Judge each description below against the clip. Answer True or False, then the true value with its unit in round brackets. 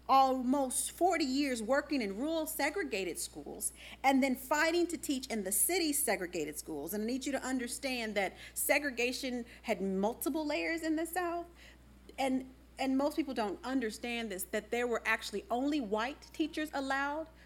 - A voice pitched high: True (270 Hz)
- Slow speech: False (160 wpm)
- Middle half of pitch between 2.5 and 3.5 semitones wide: False (4.6 semitones)